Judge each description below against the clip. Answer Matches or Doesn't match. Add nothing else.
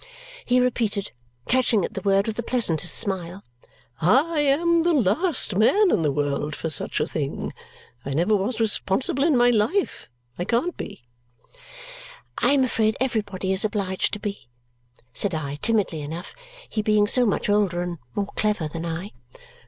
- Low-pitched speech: Doesn't match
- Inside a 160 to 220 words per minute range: Matches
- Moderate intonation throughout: Doesn't match